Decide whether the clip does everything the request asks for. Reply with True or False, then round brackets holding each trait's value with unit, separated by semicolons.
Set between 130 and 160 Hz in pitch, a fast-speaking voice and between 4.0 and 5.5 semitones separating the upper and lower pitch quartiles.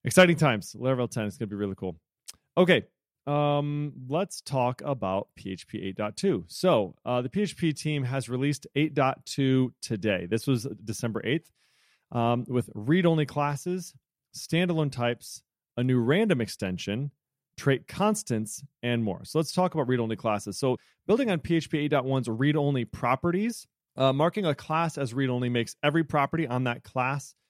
False (135 Hz; 160 wpm; 4.4 semitones)